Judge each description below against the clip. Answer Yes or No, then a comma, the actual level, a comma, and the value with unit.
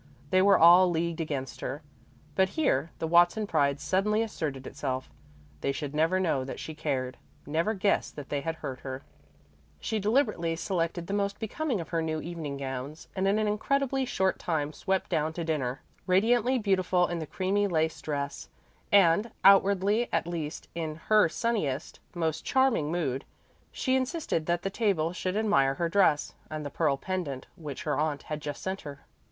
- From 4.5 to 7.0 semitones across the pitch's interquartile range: Yes, average, 5.0 semitones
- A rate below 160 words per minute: No, average, 175 wpm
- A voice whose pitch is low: No, medium, 170 Hz